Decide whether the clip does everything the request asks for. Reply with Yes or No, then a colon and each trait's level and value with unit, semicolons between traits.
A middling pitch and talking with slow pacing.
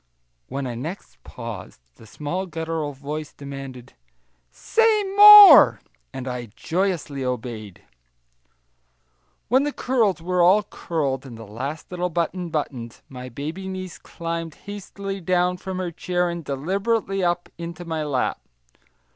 Yes: medium, 165 Hz; slow, 130 wpm